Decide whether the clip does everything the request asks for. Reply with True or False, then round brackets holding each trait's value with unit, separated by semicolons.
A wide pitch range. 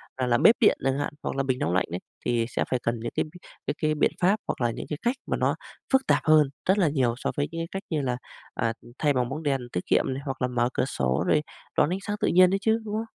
True (6.5 semitones)